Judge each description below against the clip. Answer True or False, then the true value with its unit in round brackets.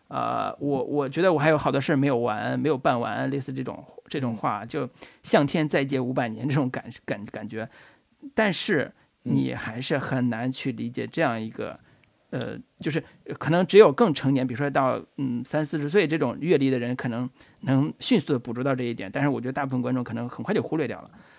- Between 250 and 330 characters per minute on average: True (305 characters per minute)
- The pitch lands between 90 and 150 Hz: True (135 Hz)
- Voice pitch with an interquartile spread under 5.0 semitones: True (2.9 semitones)